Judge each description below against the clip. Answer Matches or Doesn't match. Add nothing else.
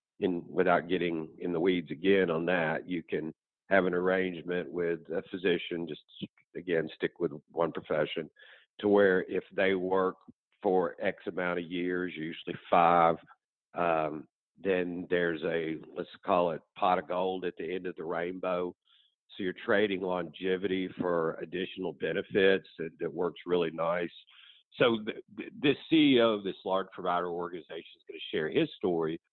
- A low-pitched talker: Matches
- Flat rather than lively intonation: Matches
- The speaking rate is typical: Matches